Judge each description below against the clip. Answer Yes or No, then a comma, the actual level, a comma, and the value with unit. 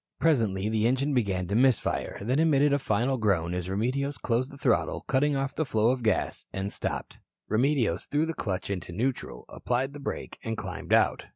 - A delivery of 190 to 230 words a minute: Yes, average, 195 wpm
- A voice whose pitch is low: Yes, low, 120 Hz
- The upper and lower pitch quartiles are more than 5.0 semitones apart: Yes, wide, 5.5 semitones